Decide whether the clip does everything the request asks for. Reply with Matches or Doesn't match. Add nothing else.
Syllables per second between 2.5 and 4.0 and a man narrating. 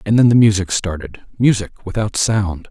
Doesn't match